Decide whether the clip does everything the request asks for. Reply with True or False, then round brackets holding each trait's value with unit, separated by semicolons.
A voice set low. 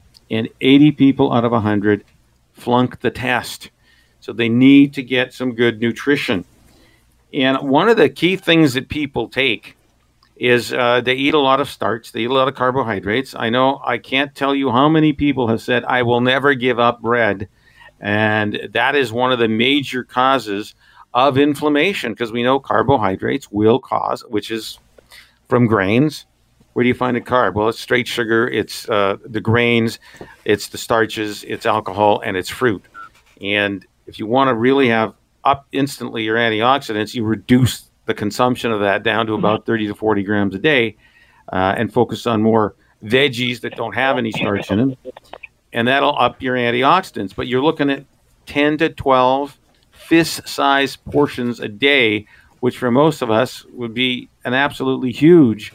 True (120 Hz)